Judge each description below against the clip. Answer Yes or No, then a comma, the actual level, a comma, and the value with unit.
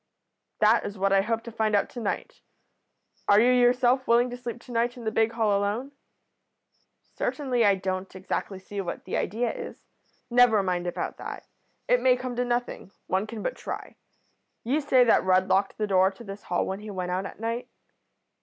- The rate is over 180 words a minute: Yes, average, 200 wpm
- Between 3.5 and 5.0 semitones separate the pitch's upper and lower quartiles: Yes, average, 3.9 semitones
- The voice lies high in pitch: Yes, high, 220 Hz